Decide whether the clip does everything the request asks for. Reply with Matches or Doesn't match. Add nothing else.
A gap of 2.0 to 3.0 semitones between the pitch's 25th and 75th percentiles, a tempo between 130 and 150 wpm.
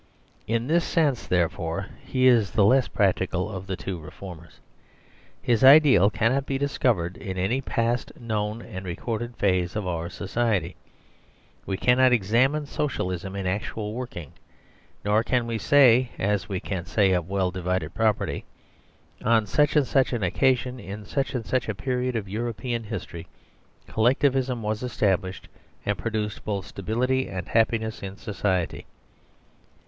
Doesn't match